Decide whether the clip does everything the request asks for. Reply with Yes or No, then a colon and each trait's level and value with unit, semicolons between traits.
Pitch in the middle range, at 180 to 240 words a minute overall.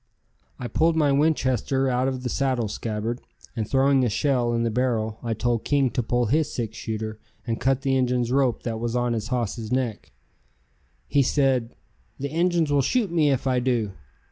No: low, 125 Hz; average, 190 wpm